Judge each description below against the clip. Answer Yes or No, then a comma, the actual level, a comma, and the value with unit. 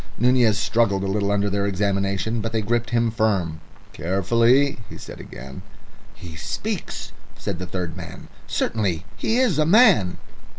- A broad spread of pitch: No, average, 3.7 semitones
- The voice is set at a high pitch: No, low, 105 Hz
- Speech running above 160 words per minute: No, average, 155 wpm